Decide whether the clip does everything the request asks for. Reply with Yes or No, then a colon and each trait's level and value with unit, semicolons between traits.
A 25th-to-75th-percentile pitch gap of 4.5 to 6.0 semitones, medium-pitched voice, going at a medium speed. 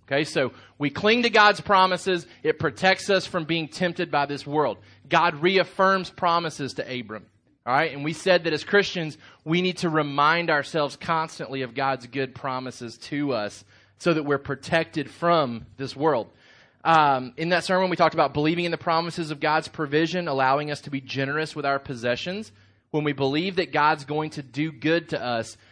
No: average, 4.0 semitones; medium, 155 Hz; average, 190 wpm